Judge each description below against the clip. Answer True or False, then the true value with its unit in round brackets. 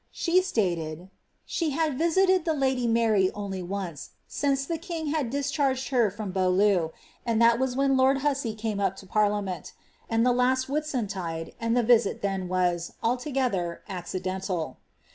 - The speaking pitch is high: True (230 Hz)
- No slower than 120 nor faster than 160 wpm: True (155 wpm)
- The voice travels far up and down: True (6.3 semitones)